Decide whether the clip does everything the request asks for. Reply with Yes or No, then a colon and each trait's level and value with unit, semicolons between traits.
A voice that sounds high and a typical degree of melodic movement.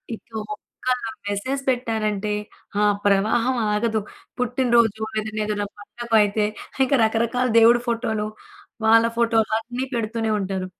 No: high, 225 Hz; narrow, 2.1 semitones